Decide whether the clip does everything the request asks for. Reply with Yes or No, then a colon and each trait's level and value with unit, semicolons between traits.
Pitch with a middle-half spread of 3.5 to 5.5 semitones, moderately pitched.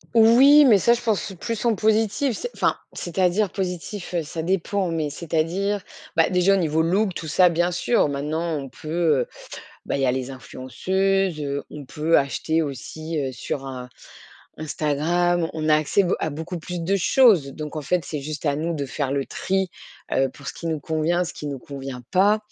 Yes: average, 4.5 semitones; medium, 165 Hz